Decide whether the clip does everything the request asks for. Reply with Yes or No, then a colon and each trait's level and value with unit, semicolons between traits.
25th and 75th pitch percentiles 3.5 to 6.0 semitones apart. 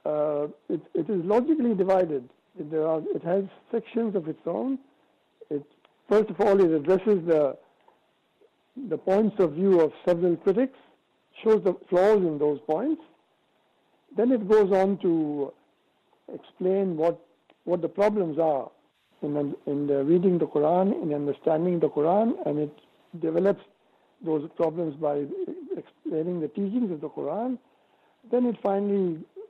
Yes: average, 5.1 semitones